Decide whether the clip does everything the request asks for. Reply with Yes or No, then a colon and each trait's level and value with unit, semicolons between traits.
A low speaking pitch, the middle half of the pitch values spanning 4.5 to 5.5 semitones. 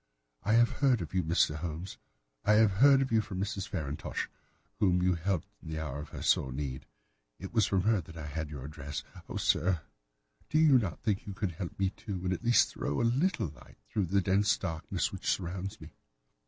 Yes: very low, 95 Hz; average, 5.1 semitones